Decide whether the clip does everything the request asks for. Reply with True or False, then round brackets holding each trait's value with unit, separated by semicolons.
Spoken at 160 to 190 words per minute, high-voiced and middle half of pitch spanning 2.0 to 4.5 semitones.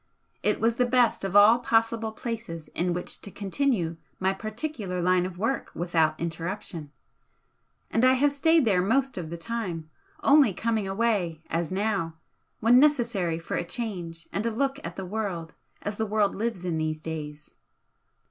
False (165 wpm; 200 Hz; 5.3 semitones)